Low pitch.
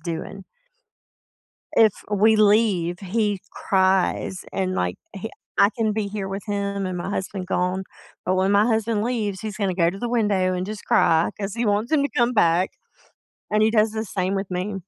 No: high, 200 Hz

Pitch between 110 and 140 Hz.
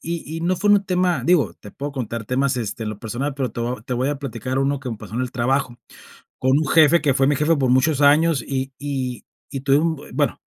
Yes: low, 135 Hz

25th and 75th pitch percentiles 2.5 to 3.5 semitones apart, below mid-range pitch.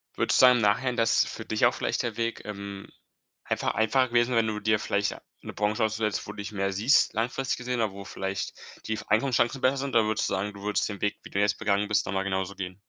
Yes: average, 2.8 semitones; low, 105 Hz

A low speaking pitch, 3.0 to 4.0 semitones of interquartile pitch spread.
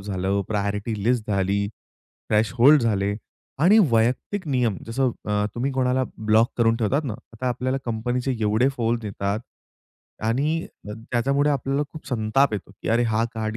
Yes: low, 115 Hz; average, 3.4 semitones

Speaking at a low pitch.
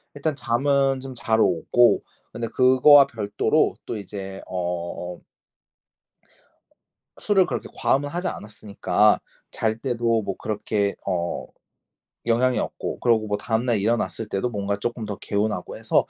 Yes: low, 115 Hz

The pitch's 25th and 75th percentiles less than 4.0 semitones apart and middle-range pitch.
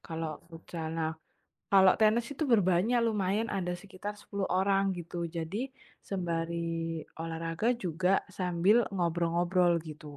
Yes: average, 3.2 semitones; medium, 180 Hz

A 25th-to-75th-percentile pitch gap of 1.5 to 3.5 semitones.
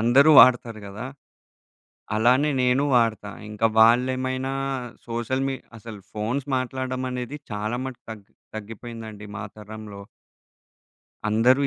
Yes: average, 2.9 semitones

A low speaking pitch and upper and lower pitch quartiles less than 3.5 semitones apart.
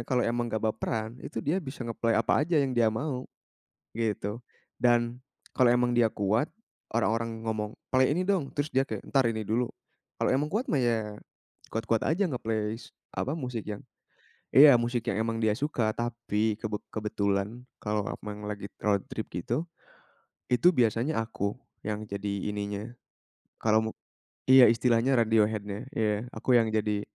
Yes: low, 115 Hz; average, 2.8 semitones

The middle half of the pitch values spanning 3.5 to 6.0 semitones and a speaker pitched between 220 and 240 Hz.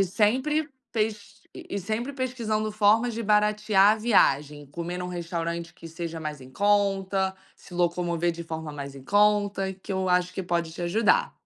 No: average, 3.8 semitones; high, 190 Hz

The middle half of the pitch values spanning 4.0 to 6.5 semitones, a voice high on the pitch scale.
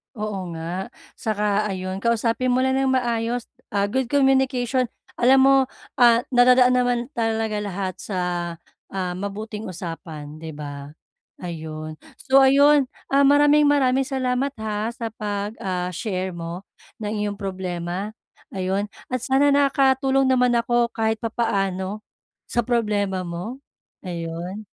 Yes: average, 5.3 semitones; high, 220 Hz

